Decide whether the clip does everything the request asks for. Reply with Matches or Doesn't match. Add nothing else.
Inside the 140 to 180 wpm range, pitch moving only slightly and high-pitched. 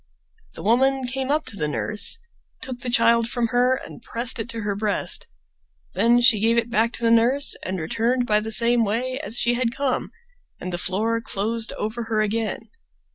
Doesn't match